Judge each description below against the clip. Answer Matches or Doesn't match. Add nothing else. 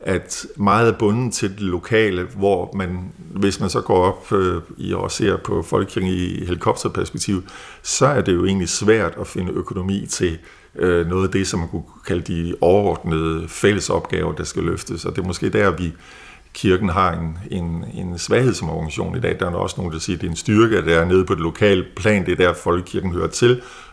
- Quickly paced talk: Doesn't match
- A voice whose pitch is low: Matches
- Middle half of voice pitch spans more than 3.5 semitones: Doesn't match